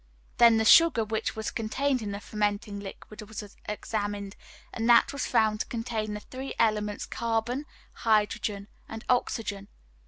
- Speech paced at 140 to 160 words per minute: Yes, average, 150 wpm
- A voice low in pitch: No, high, 220 Hz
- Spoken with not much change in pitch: Yes, narrow, 2.0 semitones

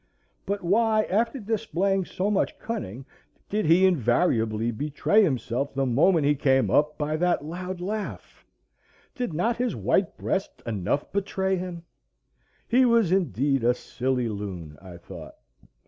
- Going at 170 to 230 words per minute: No, average, 140 wpm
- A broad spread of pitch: Yes, wide, 7.3 semitones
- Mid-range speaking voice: Yes, medium, 170 Hz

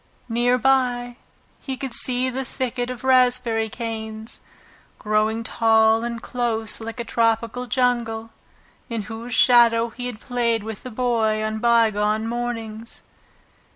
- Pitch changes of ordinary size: No, narrow, 1.8 semitones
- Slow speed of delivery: Yes, slow, 130 wpm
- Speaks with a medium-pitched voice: No, high, 230 Hz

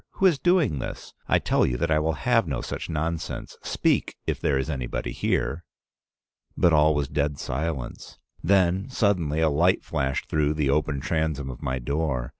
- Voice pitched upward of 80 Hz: No, very low, 75 Hz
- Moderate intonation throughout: Yes, average, 3.2 semitones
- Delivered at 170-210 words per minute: Yes, average, 175 wpm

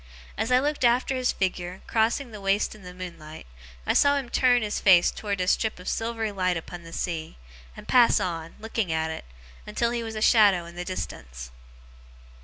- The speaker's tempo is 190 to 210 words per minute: Yes, average, 200 wpm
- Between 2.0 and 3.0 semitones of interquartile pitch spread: No, average, 4.8 semitones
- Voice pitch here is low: No, high, 200 Hz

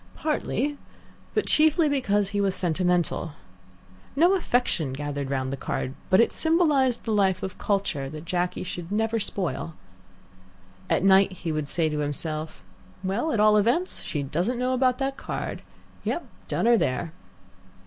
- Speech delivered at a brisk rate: No, average, 155 wpm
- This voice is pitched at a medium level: No, high, 195 Hz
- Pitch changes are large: Yes, wide, 7.7 semitones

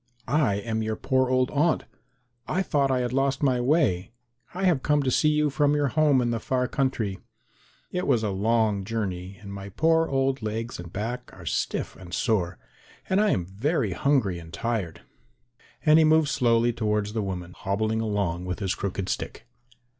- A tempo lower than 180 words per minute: No, average, 185 wpm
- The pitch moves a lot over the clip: Yes, wide, 5.8 semitones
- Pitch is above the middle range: No, low, 115 Hz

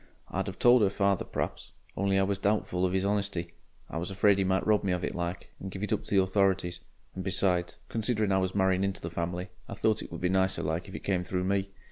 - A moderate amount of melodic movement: No, narrow, 1.7 semitones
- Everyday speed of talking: No, fast, 255 wpm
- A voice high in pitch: No, very low, 95 Hz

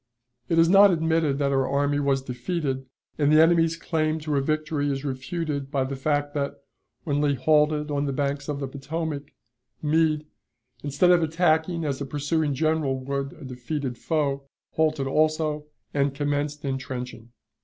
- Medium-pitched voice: Yes, medium, 145 Hz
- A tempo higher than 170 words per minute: No, average, 165 wpm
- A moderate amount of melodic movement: No, narrow, 2.3 semitones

